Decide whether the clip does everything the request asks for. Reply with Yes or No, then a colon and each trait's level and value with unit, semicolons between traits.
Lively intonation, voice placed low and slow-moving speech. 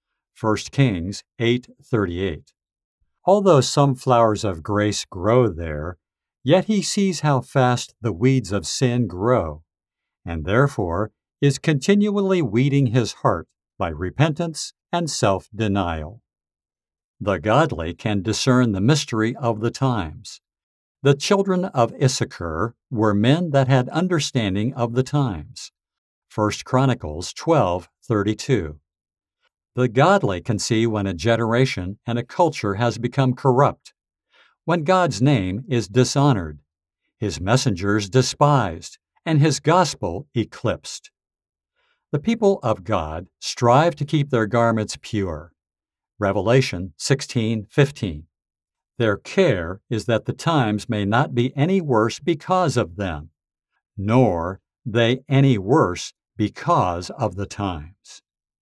Yes: wide, 6.1 semitones; low, 115 Hz; slow, 115 wpm